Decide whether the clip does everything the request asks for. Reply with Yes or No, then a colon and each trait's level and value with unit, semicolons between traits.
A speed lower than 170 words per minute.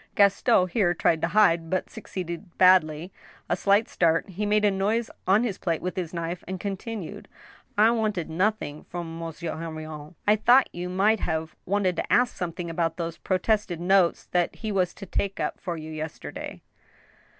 No: average, 175 wpm